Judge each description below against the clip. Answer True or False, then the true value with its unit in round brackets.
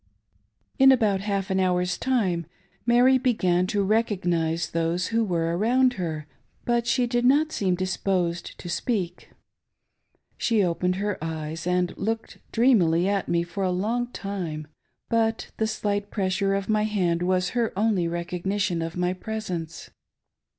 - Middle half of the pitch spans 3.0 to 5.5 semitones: True (4.1 semitones)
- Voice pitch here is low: False (190 Hz)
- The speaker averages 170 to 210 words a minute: False (150 wpm)